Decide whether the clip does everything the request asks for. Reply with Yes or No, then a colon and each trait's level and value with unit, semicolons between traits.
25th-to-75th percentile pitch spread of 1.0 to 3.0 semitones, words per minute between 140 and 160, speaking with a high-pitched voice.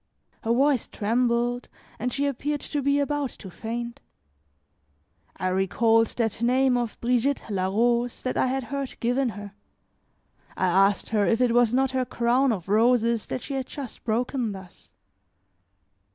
Yes: average, 2.7 semitones; average, 155 wpm; high, 240 Hz